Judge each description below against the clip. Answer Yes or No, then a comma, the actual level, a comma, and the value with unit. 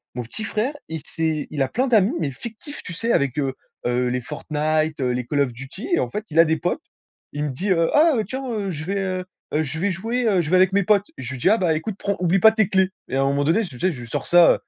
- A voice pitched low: No, medium, 170 Hz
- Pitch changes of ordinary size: No, wide, 6.2 semitones